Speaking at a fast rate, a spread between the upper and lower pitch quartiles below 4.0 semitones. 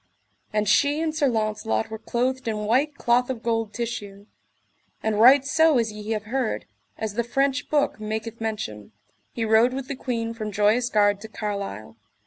No: average, 175 wpm; average, 3.3 semitones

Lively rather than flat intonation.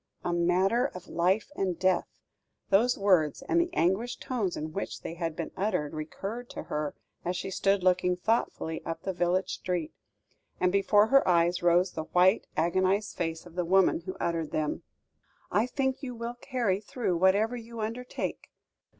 No: average, 4.2 semitones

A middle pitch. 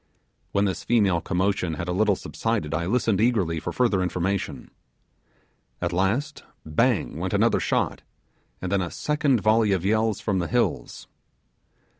No: low, 100 Hz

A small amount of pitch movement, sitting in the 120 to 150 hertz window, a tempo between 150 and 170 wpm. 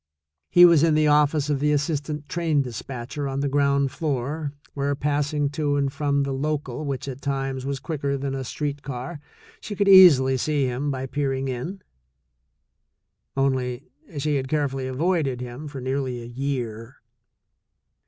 Yes: narrow, 2.0 semitones; medium, 140 Hz; average, 160 wpm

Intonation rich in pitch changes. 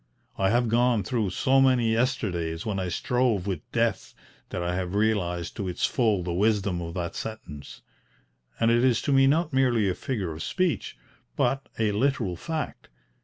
Yes: wide, 5.7 semitones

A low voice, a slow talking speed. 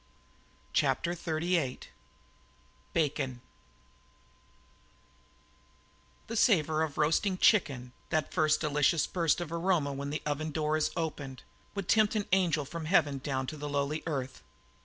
No: medium, 155 Hz; slow, 125 wpm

